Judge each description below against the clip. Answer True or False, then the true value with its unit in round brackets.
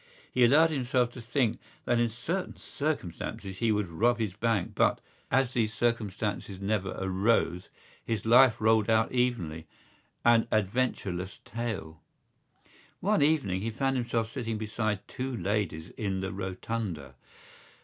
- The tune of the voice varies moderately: True (3.9 semitones)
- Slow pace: True (130 wpm)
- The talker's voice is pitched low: True (110 Hz)